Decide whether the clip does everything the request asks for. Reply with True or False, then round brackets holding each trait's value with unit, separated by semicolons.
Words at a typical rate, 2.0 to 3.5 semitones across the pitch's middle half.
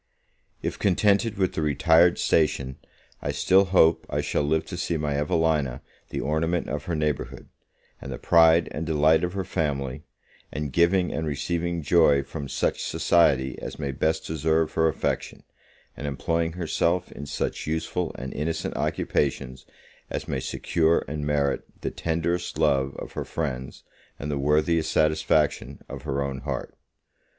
True (155 wpm; 2.7 semitones)